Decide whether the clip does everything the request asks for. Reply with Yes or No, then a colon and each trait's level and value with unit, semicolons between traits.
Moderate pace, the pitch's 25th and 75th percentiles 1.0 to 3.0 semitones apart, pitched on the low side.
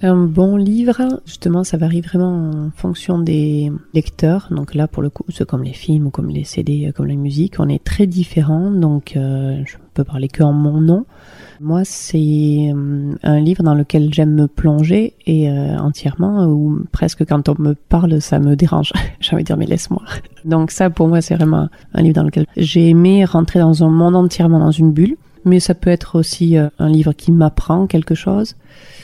No: average, 205 wpm; average, 2.7 semitones; medium, 160 Hz